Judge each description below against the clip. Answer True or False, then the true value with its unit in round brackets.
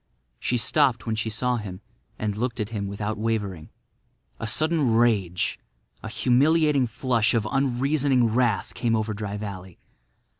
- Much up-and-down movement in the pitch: False (3.3 semitones)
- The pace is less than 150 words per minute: True (135 wpm)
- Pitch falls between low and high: False (115 Hz)